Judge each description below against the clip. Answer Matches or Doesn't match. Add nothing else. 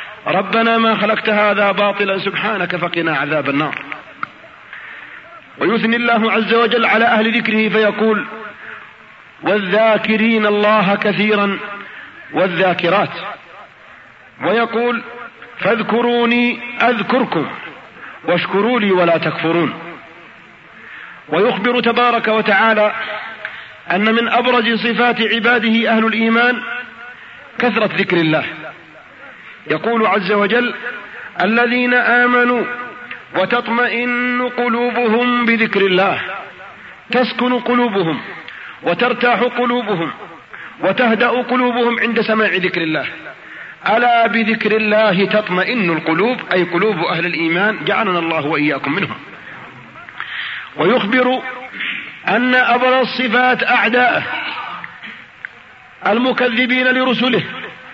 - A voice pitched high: Matches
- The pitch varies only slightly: Doesn't match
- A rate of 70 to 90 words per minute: Matches